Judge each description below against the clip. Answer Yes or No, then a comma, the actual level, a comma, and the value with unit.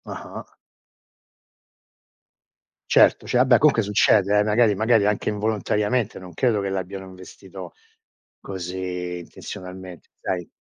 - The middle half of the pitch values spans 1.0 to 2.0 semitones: No, average, 2.8 semitones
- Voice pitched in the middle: No, low, 100 Hz